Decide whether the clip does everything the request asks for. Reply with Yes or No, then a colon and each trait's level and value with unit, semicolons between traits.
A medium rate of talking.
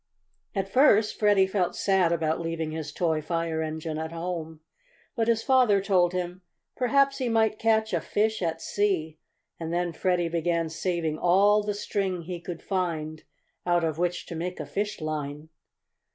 Yes: average, 165 wpm